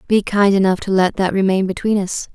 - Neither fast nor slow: No, fast, 230 wpm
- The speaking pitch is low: No, high, 195 Hz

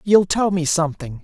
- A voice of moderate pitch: Yes, medium, 175 Hz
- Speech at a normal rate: Yes, average, 195 wpm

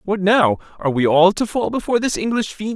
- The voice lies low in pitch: No, high, 200 Hz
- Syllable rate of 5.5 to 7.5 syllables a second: Yes, 5.8 syllables/s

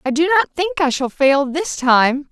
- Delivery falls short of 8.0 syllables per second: Yes, 4.1 syllables/s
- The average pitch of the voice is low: No, very high, 300 Hz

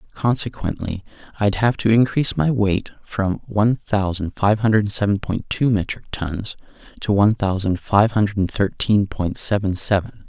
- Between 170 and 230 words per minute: No, average, 150 wpm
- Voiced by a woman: No, male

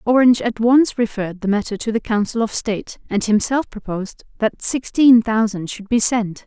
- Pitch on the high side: Yes, high, 225 Hz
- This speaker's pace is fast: No, average, 185 wpm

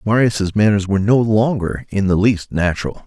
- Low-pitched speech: Yes, low, 105 Hz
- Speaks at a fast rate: No, average, 175 wpm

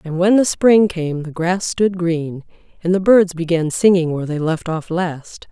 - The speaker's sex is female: Yes, female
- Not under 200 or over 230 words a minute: Yes, fast, 205 wpm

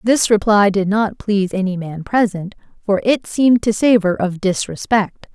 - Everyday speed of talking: Yes, average, 170 wpm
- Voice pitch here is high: Yes, high, 205 Hz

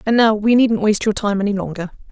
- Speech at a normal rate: No, fast, 255 wpm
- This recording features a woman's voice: Yes, female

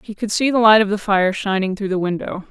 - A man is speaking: No, female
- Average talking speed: No, fast, 290 wpm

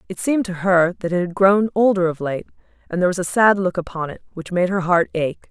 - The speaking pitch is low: No, medium, 180 Hz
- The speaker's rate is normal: No, fast, 260 wpm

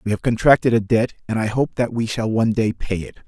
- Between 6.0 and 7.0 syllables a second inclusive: Yes, 6.1 syllables/s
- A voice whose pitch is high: No, low, 115 Hz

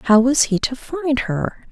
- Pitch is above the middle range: Yes, very high, 250 Hz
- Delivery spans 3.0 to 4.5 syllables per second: Yes, 3.6 syllables/s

